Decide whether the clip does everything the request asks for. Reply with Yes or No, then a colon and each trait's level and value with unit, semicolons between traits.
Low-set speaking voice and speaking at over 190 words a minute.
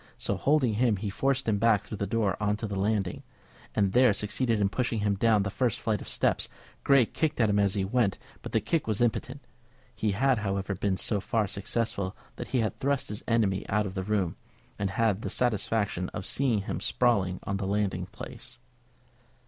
Yes: low, 105 Hz; fast, 205 wpm